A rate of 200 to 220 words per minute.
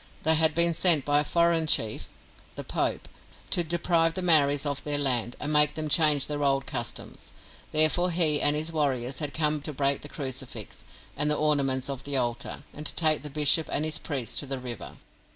Yes: fast, 205 wpm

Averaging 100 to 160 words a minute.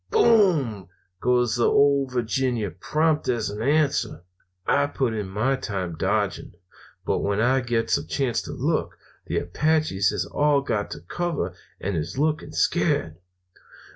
Yes: average, 145 wpm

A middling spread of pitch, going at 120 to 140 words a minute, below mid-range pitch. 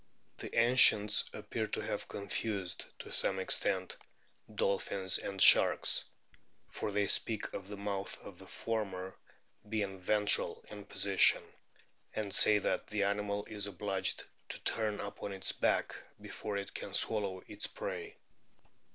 No: narrow, 1.5 semitones; slow, 135 wpm; low, 100 Hz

